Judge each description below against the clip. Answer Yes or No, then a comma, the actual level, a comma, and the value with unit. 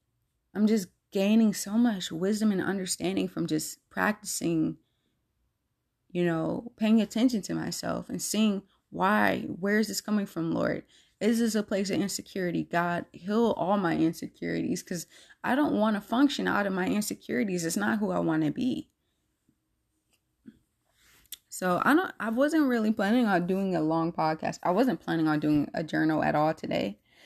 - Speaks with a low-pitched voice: No, high, 200 Hz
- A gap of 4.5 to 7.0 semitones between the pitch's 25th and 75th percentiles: Yes, average, 4.8 semitones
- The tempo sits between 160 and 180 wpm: Yes, average, 165 wpm